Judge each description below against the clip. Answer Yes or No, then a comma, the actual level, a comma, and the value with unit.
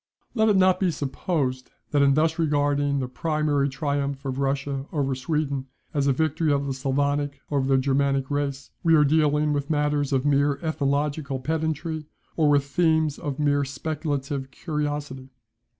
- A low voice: No, medium, 145 Hz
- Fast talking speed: No, average, 165 wpm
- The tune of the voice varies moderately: No, narrow, 1.8 semitones